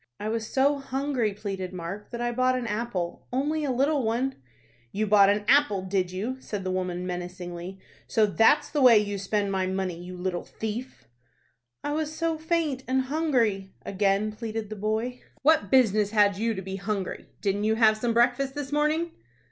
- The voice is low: No, high, 220 Hz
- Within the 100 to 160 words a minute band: No, average, 185 wpm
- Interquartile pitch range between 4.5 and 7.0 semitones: Yes, average, 5.1 semitones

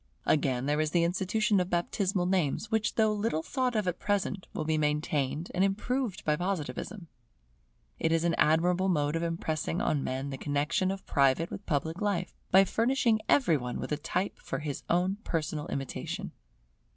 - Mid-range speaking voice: Yes, medium, 175 Hz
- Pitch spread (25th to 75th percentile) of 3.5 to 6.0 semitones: Yes, average, 4.5 semitones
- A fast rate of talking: No, average, 175 wpm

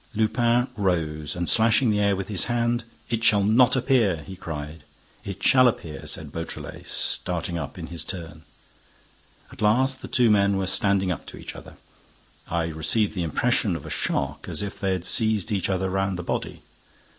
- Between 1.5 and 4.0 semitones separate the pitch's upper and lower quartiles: No, average, 4.4 semitones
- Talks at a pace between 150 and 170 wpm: No, average, 185 wpm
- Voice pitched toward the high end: No, low, 100 Hz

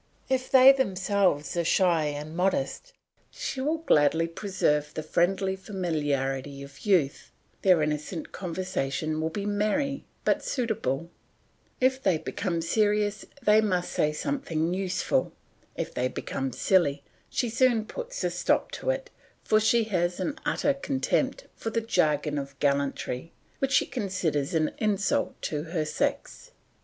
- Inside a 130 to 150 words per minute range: Yes, average, 140 wpm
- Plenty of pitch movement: Yes, wide, 6.4 semitones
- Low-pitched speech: No, medium, 185 Hz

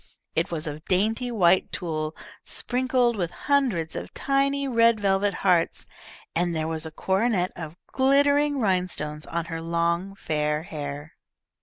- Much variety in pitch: Yes, wide, 6.5 semitones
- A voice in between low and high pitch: Yes, medium, 180 Hz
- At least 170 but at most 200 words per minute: No, average, 140 wpm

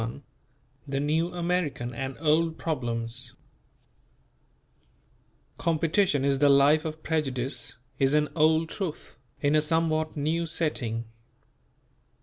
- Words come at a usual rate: No, slow, 110 wpm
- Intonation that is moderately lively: Yes, average, 3.2 semitones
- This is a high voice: No, medium, 150 Hz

